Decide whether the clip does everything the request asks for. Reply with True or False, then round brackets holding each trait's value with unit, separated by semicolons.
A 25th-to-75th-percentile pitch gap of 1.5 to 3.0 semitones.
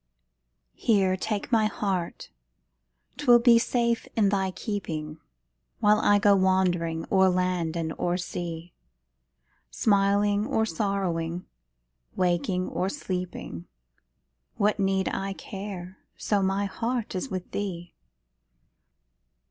True (2.6 semitones)